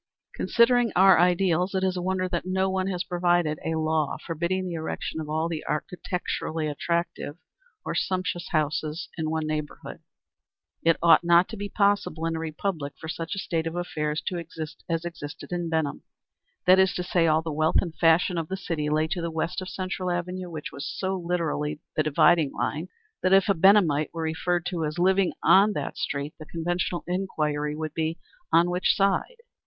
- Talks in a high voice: No, medium, 170 Hz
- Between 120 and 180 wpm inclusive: No, average, 190 wpm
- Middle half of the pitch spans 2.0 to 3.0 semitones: Yes, average, 2.7 semitones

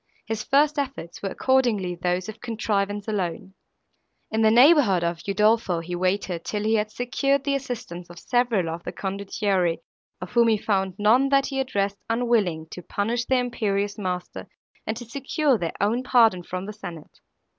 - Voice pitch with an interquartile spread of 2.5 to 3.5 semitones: No, average, 4.8 semitones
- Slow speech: No, average, 170 wpm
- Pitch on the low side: No, high, 210 Hz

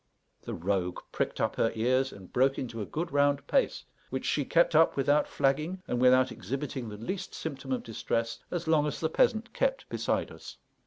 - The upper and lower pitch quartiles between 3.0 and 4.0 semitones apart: No, average, 5.1 semitones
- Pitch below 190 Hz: Yes, low, 135 Hz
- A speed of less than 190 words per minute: No, average, 195 wpm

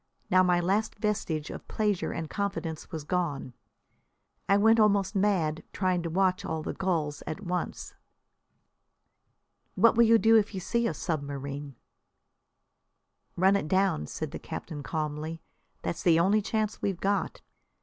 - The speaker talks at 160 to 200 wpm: No, average, 150 wpm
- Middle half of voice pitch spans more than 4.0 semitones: Yes, average, 4.4 semitones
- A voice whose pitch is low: No, medium, 185 Hz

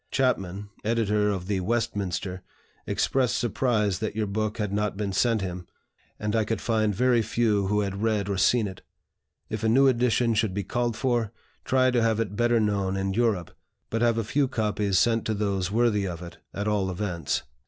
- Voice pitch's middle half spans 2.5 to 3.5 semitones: Yes, average, 2.9 semitones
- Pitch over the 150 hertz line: No, low, 105 Hz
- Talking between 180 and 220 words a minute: Yes, average, 195 wpm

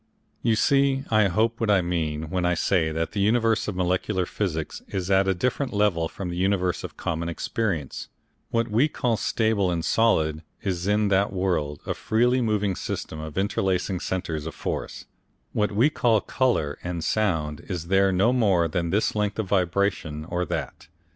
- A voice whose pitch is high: No, very low, 95 Hz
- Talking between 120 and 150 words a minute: No, average, 180 wpm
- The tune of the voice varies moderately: Yes, average, 4.0 semitones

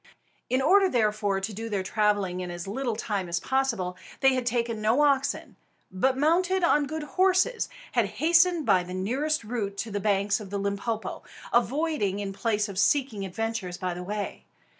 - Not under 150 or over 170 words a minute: No, average, 180 wpm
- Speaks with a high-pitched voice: Yes, high, 220 Hz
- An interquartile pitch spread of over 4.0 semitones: Yes, wide, 5.5 semitones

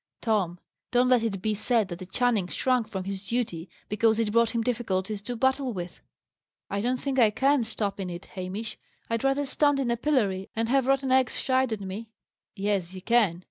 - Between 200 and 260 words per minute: Yes, fast, 205 wpm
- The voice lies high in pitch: Yes, high, 225 Hz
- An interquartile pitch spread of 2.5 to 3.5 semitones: No, average, 4.4 semitones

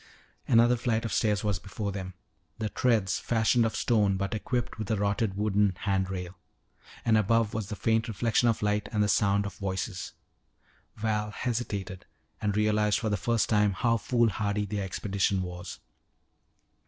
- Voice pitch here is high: No, low, 105 Hz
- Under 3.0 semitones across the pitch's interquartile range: Yes, narrow, 2.4 semitones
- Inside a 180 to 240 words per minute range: No, average, 165 wpm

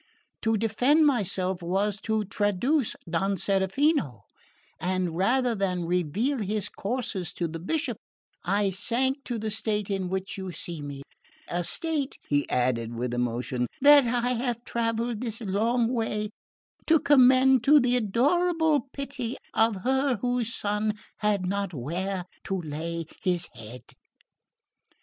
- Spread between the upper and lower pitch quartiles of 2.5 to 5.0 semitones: No, wide, 5.4 semitones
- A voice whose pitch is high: Yes, high, 210 Hz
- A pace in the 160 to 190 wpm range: No, slow, 135 wpm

